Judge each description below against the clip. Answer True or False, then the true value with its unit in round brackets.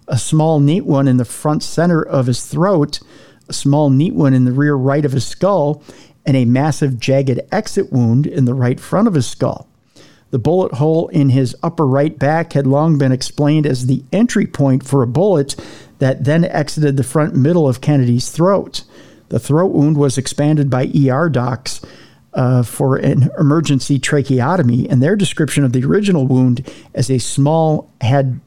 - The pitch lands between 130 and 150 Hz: True (140 Hz)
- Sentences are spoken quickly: False (185 wpm)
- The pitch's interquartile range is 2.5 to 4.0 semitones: True (2.9 semitones)